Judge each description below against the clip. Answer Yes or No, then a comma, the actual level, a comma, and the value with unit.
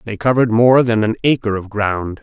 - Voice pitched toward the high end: No, low, 110 Hz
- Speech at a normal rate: No, fast, 215 wpm